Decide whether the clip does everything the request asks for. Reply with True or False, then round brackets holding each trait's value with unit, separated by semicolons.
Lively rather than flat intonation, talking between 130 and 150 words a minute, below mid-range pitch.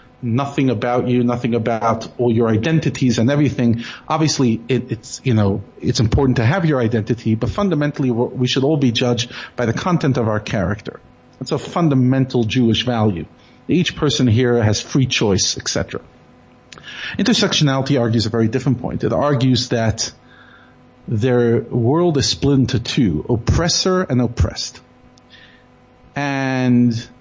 False (2.8 semitones; 145 wpm; 125 Hz)